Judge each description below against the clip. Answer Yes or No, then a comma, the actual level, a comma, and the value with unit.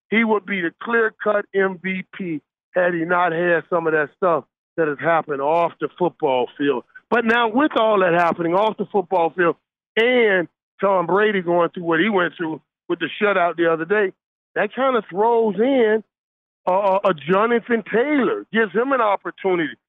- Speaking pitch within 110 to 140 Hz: No, high, 190 Hz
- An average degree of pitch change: Yes, average, 4.5 semitones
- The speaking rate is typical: Yes, average, 180 wpm